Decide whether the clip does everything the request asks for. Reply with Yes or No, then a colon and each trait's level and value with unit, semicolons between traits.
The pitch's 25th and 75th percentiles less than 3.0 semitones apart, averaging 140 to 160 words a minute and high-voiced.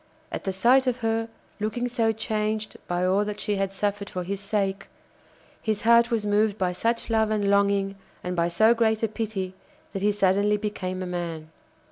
No: narrow, 2.4 semitones; average, 190 wpm; high, 205 Hz